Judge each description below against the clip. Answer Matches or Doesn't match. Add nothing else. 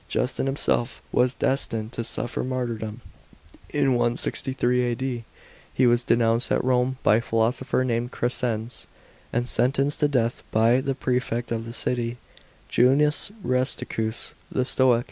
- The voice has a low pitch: Matches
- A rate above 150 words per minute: Doesn't match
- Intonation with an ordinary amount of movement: Doesn't match